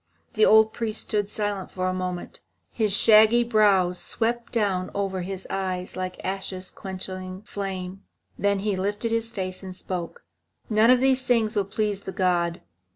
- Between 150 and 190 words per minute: Yes, average, 160 wpm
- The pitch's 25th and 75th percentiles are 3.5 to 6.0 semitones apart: No, average, 2.7 semitones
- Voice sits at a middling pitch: No, high, 195 Hz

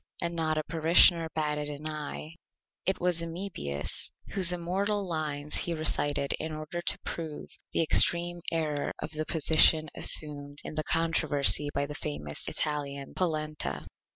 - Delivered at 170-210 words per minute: No, average, 145 wpm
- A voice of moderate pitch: Yes, medium, 155 Hz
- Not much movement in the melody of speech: Yes, narrow, 2.3 semitones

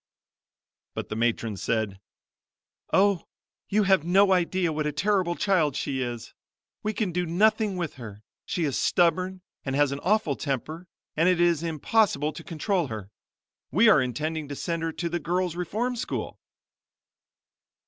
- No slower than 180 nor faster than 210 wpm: No, average, 160 wpm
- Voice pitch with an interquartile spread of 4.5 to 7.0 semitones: Yes, average, 4.8 semitones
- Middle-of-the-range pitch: Yes, medium, 170 Hz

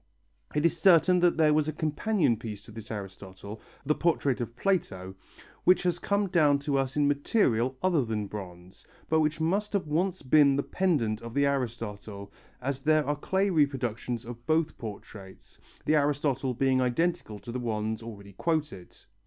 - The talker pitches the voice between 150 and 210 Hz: No, low, 135 Hz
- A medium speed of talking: Yes, average, 170 wpm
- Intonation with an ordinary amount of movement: No, wide, 6.1 semitones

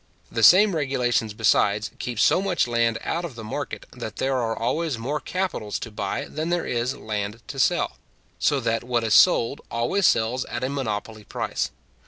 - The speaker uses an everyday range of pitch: Yes, average, 4.2 semitones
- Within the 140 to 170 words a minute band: No, average, 185 wpm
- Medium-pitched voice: No, low, 120 Hz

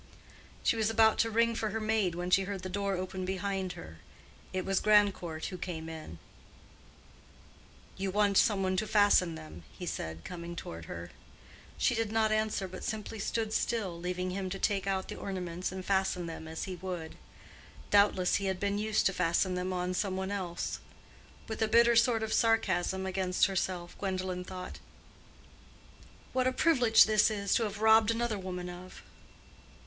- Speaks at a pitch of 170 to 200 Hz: Yes, high, 190 Hz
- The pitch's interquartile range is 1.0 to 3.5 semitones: Yes, average, 3.0 semitones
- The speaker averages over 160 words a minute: Yes, average, 180 wpm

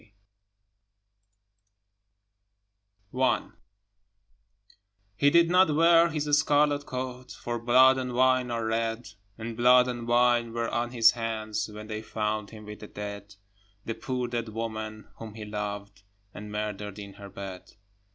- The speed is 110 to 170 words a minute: Yes, average, 140 wpm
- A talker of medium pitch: No, low, 115 Hz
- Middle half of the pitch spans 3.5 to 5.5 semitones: No, average, 3.0 semitones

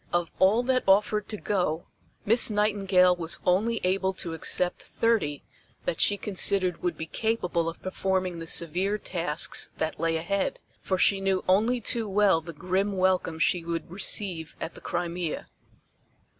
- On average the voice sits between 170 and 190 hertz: Yes, medium, 185 Hz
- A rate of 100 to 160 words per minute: Yes, average, 155 wpm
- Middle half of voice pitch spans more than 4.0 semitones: No, average, 3.2 semitones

